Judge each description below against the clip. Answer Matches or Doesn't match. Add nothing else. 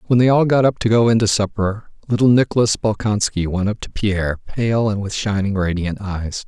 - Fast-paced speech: Matches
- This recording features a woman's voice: Doesn't match